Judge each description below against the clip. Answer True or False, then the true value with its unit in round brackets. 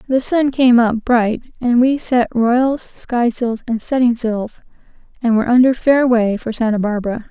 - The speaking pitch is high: True (240 Hz)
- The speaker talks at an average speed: True (170 wpm)